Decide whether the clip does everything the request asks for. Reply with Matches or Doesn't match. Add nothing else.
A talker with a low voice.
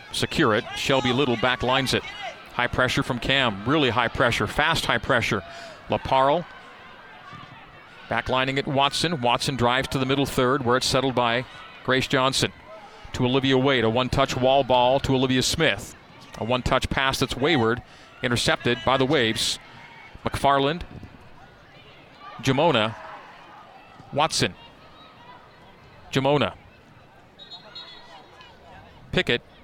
Matches